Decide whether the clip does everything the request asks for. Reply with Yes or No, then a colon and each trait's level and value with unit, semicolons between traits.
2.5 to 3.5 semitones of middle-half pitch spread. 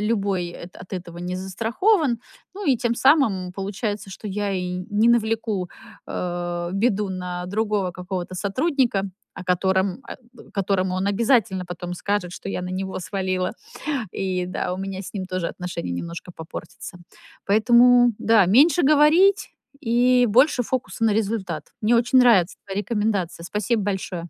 No: average, 4.2 semitones